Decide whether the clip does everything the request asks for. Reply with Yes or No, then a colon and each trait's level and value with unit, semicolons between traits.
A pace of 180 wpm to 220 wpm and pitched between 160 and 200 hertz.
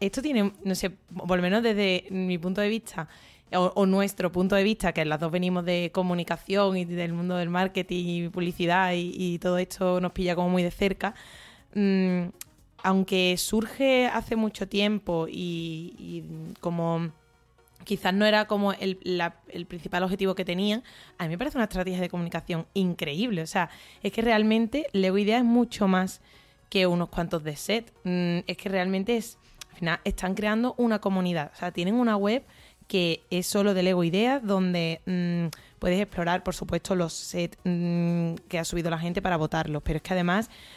Yes: average, 185 wpm; medium, 185 Hz